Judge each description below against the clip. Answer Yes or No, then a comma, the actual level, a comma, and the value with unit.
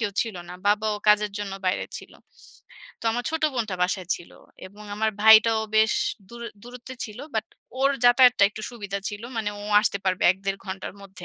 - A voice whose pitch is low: No, high, 215 Hz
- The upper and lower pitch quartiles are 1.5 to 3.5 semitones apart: Yes, average, 2.7 semitones